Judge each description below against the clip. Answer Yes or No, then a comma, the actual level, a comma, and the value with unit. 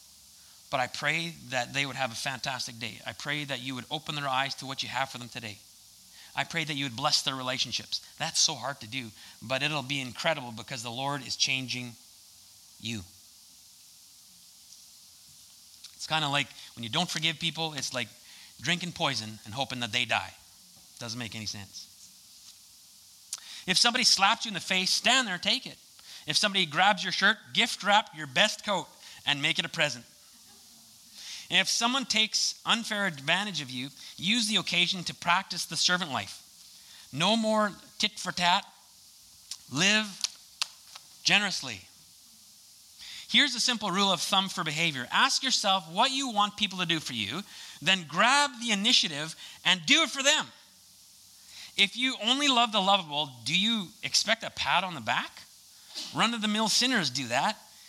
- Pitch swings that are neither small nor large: No, wide, 8.0 semitones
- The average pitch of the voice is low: No, medium, 160 Hz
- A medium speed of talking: Yes, average, 175 wpm